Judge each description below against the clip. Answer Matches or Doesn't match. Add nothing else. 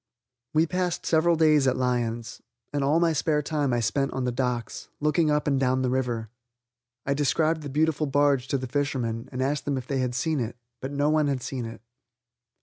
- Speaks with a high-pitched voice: Doesn't match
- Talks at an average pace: Doesn't match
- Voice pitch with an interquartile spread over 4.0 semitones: Doesn't match